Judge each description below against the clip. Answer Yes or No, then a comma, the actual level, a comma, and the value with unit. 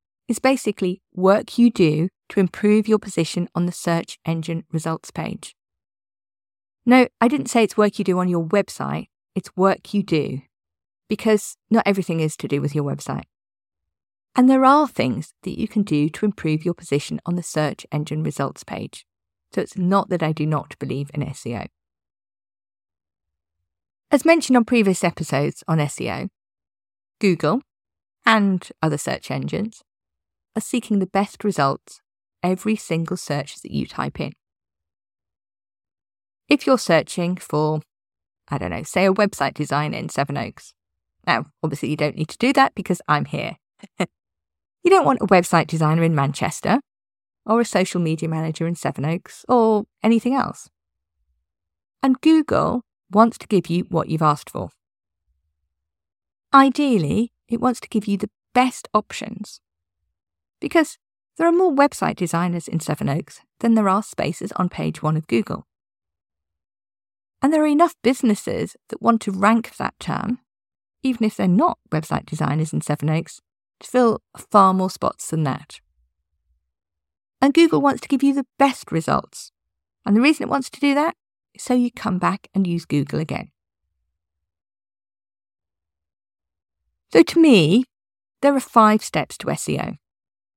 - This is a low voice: No, medium, 170 Hz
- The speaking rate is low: No, average, 155 wpm